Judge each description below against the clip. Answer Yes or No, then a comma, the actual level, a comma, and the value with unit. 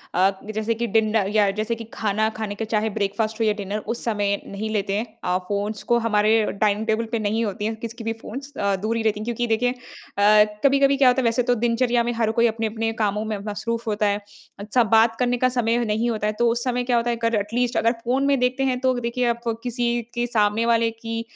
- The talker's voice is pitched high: Yes, high, 225 Hz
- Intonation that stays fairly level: Yes, narrow, 2.1 semitones